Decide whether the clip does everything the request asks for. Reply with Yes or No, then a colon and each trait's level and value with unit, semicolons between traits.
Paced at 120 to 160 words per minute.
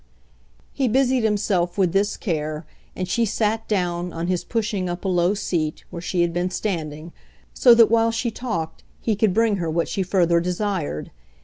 No: average, 185 wpm